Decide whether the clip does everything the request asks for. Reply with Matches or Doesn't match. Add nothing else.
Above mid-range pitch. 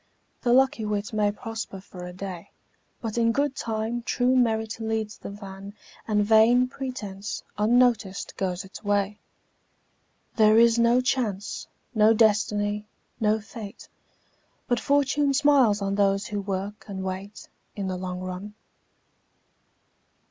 Matches